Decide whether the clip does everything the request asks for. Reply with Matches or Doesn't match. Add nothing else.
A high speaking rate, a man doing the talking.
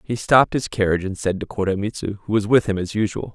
Matches